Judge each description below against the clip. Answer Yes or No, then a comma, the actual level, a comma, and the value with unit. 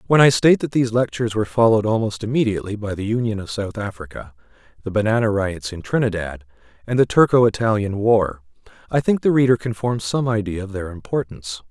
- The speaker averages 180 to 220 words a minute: Yes, average, 190 wpm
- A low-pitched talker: Yes, low, 110 Hz